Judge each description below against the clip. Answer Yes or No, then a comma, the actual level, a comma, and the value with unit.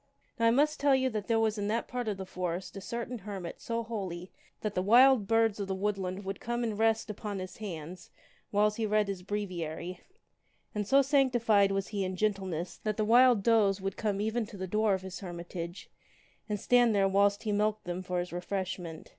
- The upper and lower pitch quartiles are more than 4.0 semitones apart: No, average, 3.1 semitones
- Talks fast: Yes, fast, 215 wpm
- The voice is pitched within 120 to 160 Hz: No, high, 205 Hz